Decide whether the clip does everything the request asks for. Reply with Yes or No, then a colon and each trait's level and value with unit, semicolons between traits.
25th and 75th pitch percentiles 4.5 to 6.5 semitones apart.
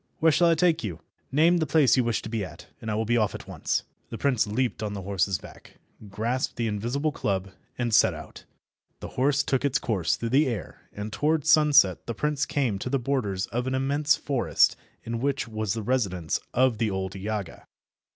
Yes: average, 5.2 semitones